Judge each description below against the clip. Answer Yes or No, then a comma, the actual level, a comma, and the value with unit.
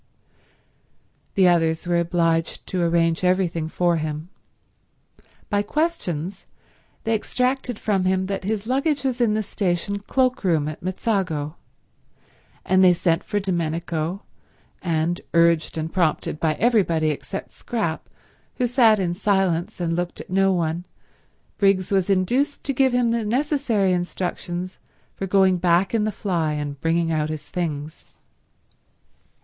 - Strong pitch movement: No, average, 3.9 semitones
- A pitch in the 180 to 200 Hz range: Yes, medium, 185 Hz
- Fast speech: No, slow, 135 wpm